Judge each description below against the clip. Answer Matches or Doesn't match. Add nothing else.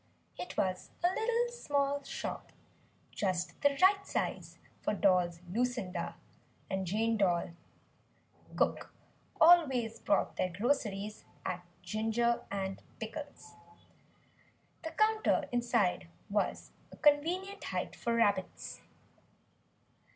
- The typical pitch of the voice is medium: Doesn't match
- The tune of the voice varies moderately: Doesn't match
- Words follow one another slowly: Matches